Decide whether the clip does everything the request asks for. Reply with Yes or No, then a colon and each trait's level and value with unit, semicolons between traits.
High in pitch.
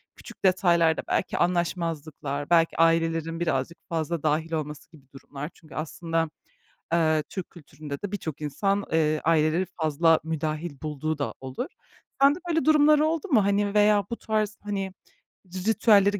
No: medium, 165 Hz